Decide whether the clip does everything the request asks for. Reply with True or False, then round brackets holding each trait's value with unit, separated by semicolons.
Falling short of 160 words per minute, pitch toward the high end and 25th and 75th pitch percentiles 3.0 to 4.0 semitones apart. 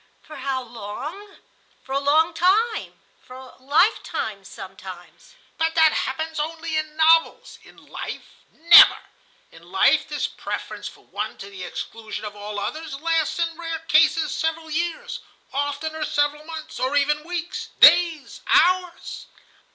True (145 wpm; 310 Hz; 3.7 semitones)